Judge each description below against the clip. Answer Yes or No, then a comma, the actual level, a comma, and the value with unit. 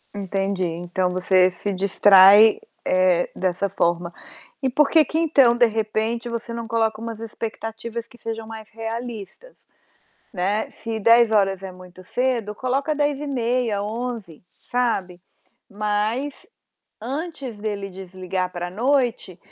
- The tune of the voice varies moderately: Yes, average, 3.9 semitones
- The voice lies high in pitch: Yes, high, 220 Hz